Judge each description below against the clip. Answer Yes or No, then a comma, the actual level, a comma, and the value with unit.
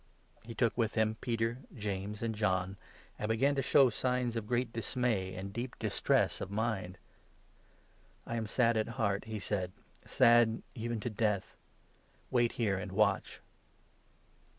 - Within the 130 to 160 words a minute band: Yes, average, 155 wpm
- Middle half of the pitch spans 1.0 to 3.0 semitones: Yes, narrow, 2.6 semitones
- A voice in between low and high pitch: No, low, 110 Hz